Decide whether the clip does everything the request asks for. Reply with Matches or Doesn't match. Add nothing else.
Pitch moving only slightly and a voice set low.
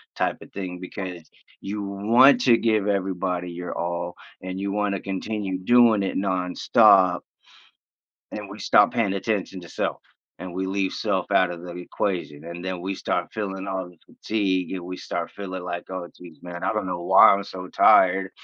Matches